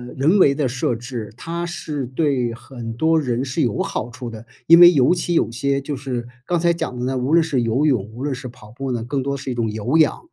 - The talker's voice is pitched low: Yes, low, 130 Hz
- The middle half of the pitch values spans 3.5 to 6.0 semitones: Yes, average, 4.0 semitones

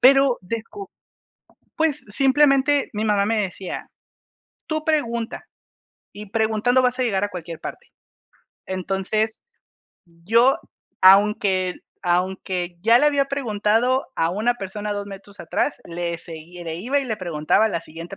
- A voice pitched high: Yes, high, 210 Hz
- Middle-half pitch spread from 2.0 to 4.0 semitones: No, average, 5.3 semitones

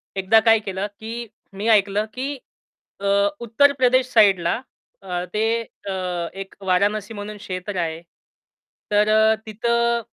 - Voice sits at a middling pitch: No, high, 210 Hz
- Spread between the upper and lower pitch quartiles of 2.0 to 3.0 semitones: Yes, narrow, 2.6 semitones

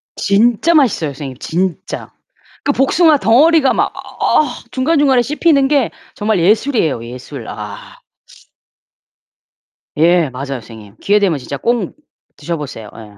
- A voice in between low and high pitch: No, high, 200 Hz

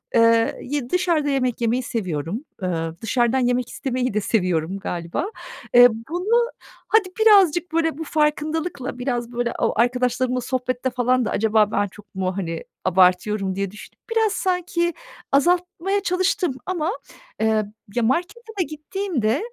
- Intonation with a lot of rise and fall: Yes, wide, 7.8 semitones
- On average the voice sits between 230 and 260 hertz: Yes, very high, 250 Hz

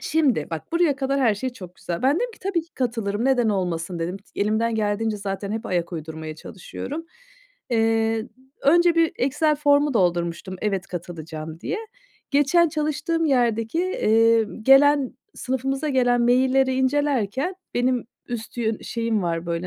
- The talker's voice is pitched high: Yes, high, 235 Hz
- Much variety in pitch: Yes, wide, 6.2 semitones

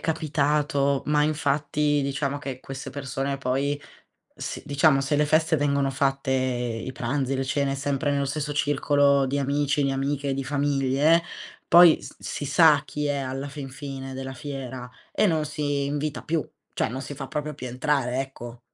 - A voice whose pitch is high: No, medium, 140 Hz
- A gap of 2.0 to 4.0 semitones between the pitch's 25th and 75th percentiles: No, narrow, 1.6 semitones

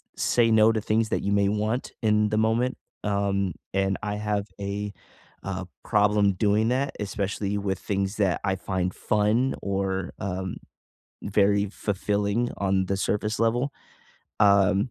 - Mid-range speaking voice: No, low, 100 Hz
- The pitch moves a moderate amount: No, narrow, 1.6 semitones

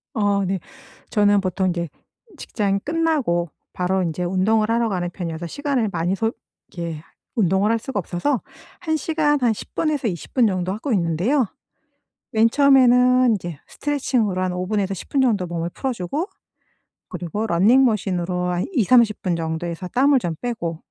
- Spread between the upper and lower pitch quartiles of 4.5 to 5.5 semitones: No, wide, 5.9 semitones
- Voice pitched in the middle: No, high, 205 Hz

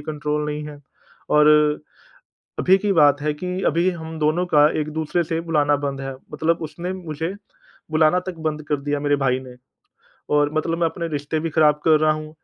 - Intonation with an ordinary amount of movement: No, narrow, 1.9 semitones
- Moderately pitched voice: Yes, medium, 155 Hz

